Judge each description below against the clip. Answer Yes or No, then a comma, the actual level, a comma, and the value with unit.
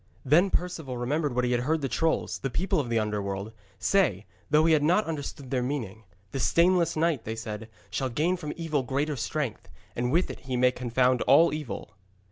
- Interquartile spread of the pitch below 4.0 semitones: No, average, 4.9 semitones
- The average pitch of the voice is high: No, low, 135 Hz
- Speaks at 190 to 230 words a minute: Yes, average, 200 wpm